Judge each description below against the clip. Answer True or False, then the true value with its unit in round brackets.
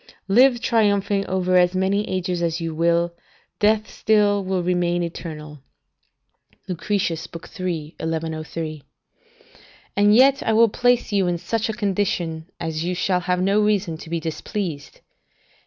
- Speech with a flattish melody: False (3.6 semitones)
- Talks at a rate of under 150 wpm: True (140 wpm)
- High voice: False (180 Hz)